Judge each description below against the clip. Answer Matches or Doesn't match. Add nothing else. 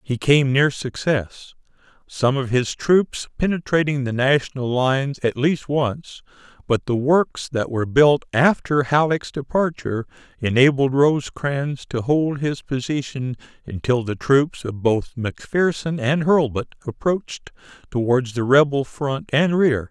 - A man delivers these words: Matches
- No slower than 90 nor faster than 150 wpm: Matches